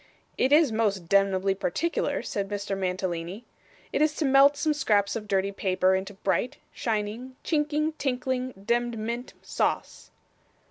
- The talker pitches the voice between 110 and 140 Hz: No, high, 215 Hz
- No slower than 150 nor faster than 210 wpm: No, average, 140 wpm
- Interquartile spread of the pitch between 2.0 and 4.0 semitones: No, average, 5.2 semitones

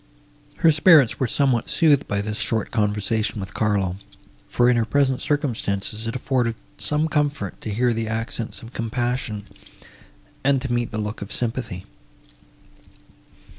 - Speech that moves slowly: No, average, 145 wpm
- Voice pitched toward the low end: Yes, low, 115 Hz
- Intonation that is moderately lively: Yes, average, 3.8 semitones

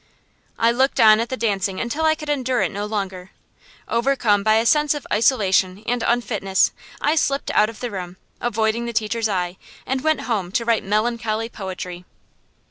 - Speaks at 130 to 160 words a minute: No, average, 180 wpm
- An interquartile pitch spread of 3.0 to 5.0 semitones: Yes, average, 3.3 semitones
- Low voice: No, high, 225 Hz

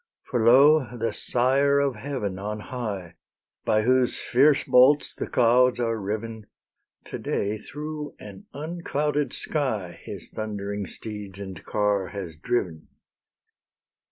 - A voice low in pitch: Yes, low, 115 Hz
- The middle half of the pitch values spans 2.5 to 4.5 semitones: No, average, 5.0 semitones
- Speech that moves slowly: Yes, slow, 125 wpm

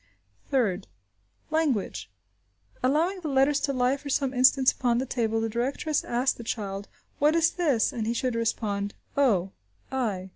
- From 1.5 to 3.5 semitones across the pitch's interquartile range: No, average, 4.0 semitones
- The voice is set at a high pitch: Yes, very high, 250 Hz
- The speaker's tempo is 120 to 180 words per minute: Yes, average, 155 wpm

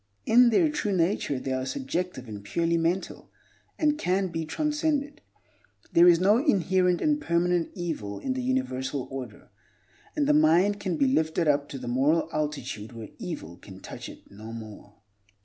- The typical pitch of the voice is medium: Yes, medium, 170 Hz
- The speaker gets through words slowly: No, average, 165 wpm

